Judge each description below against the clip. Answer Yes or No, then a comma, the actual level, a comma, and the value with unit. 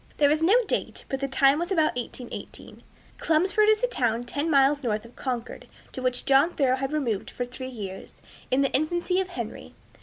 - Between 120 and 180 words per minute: No, average, 200 wpm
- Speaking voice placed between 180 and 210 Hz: No, very high, 275 Hz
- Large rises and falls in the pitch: No, average, 4.4 semitones